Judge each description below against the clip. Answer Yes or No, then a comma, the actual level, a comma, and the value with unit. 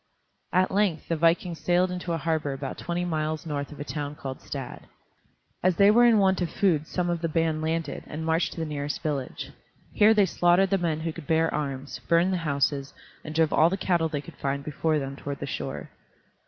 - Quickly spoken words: Yes, fast, 220 wpm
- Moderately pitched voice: Yes, medium, 160 Hz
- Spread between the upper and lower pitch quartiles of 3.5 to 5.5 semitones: No, average, 3.0 semitones